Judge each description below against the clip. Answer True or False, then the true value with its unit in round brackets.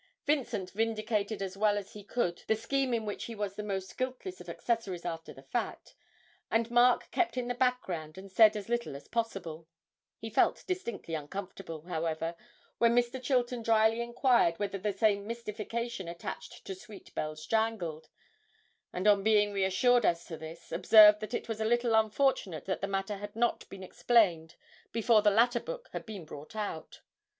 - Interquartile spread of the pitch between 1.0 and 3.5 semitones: False (3.9 semitones)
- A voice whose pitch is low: False (210 Hz)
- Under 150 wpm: False (175 wpm)